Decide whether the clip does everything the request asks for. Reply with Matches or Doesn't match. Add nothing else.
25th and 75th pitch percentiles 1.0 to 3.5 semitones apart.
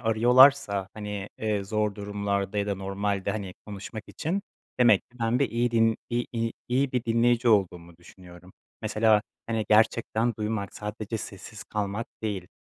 Matches